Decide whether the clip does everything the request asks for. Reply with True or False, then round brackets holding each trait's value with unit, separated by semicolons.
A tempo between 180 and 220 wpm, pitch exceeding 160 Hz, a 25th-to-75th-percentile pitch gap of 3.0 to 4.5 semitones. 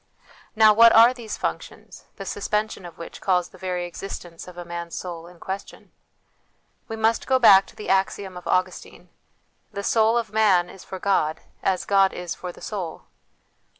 True (185 wpm; 190 Hz; 3.4 semitones)